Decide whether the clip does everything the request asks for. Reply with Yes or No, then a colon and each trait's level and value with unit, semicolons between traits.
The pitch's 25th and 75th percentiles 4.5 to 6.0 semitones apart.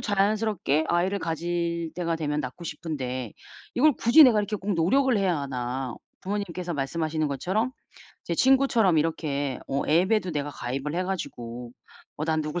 Yes: wide, 5.5 semitones